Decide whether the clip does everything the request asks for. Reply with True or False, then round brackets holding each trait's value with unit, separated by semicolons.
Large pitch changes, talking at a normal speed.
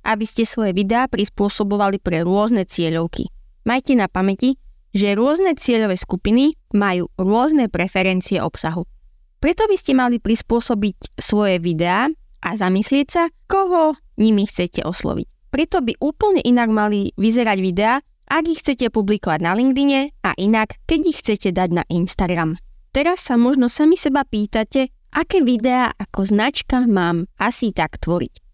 True (5.9 semitones; 145 wpm)